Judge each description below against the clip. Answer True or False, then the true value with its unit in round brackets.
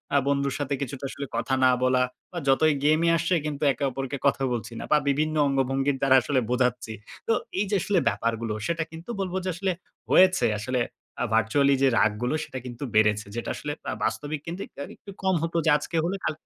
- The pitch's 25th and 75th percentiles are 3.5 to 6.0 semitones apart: True (4.3 semitones)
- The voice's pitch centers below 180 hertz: True (140 Hz)